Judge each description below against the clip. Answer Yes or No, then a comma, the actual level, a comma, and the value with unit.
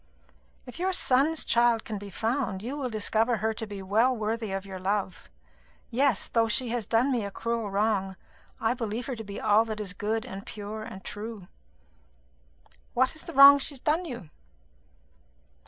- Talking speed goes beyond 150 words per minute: Yes, average, 190 wpm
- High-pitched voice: Yes, high, 225 Hz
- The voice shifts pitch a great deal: No, average, 3.4 semitones